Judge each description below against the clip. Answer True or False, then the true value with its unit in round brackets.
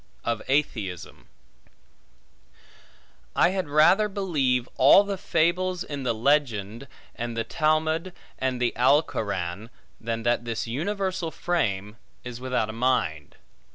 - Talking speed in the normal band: False (120 wpm)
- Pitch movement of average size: False (6.2 semitones)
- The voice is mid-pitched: False (130 Hz)